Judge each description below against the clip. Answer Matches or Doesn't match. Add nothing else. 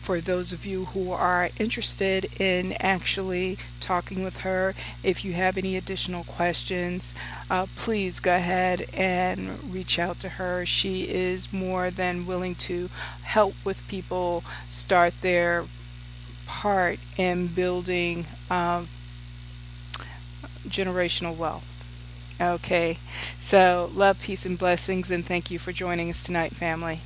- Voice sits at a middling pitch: Matches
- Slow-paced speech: Matches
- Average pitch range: Doesn't match